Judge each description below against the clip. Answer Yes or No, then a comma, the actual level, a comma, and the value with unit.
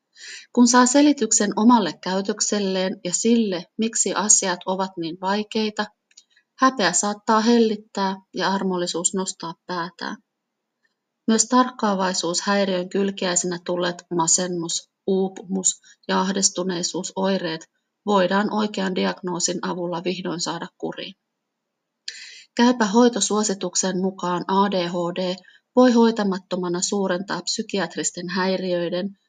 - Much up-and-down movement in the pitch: No, average, 3.0 semitones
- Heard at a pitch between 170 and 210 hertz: Yes, high, 190 Hz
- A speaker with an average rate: No, slow, 90 wpm